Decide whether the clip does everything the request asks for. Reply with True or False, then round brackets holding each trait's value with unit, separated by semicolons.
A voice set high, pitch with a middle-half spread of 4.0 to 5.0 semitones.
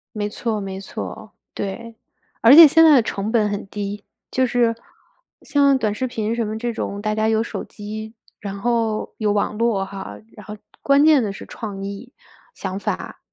False (220 Hz; 2.5 semitones)